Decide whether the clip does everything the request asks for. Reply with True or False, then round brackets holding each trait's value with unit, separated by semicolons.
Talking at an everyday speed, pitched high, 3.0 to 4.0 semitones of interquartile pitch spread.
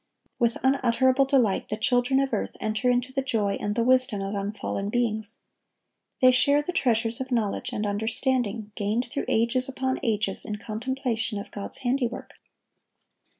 True (155 wpm; 235 Hz; 3.5 semitones)